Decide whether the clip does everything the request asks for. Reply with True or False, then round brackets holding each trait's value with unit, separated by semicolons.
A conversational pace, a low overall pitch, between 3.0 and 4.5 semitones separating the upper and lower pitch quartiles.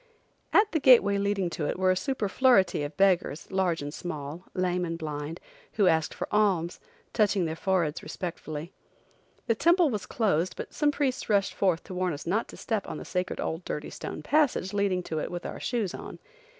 False (190 wpm; 185 Hz; 4.1 semitones)